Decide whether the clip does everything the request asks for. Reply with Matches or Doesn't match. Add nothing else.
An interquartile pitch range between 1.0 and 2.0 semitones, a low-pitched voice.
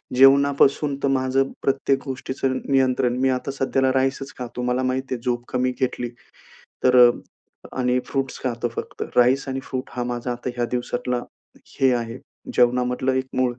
Matches